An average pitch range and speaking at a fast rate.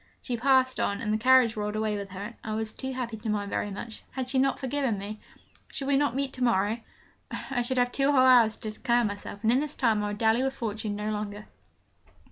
Yes: average, 3.6 semitones; fast, 245 wpm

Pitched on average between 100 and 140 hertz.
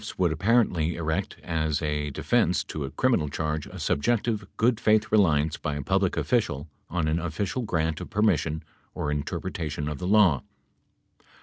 No: very low, 80 Hz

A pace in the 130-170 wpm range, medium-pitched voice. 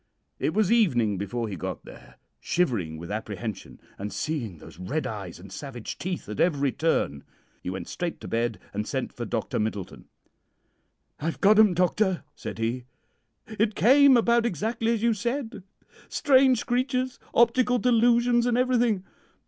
Yes: average, 155 wpm; medium, 180 Hz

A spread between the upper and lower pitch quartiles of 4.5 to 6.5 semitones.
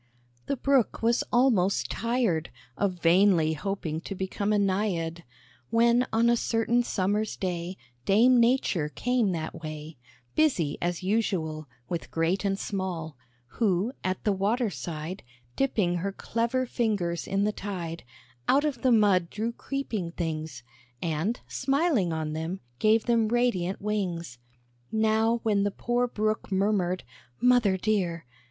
Yes: average, 5.1 semitones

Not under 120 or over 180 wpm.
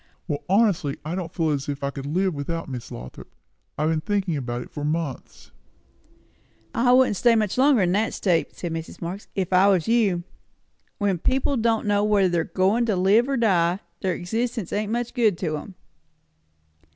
No: average, 190 wpm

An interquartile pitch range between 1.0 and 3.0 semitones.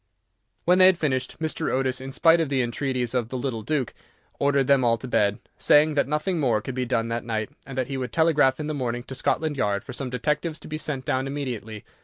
No: average, 3.5 semitones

